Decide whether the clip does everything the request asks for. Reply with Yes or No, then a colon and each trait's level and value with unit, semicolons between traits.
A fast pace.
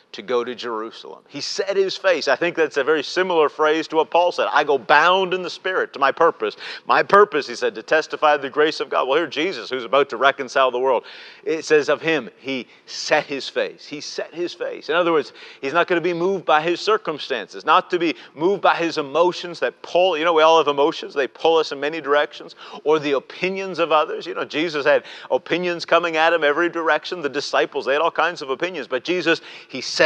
Yes: fast, 240 wpm